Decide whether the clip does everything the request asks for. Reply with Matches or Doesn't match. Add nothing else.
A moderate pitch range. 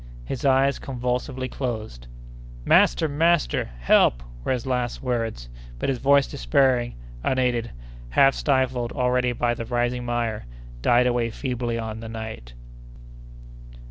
Doesn't match